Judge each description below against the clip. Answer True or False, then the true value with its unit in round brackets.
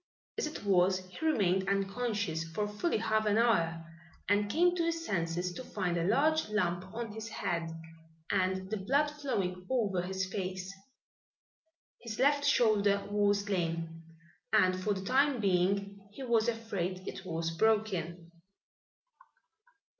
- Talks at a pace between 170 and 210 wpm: False (140 wpm)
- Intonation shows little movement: False (3.7 semitones)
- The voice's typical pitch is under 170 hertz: False (200 Hz)